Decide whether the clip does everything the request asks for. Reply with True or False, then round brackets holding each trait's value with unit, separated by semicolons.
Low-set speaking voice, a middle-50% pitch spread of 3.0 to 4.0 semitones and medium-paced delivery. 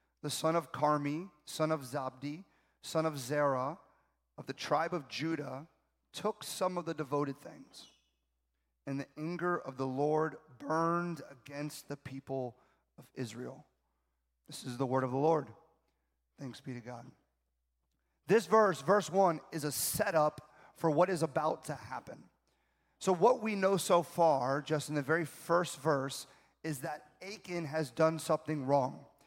False (150 Hz; 3.5 semitones; 155 wpm)